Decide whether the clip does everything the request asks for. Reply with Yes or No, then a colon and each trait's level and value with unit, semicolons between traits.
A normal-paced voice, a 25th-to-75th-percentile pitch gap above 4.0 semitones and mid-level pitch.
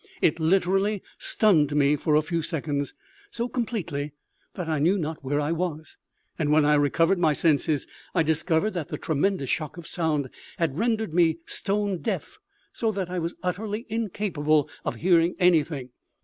Yes: average, 165 wpm; average, 4.4 semitones; medium, 165 Hz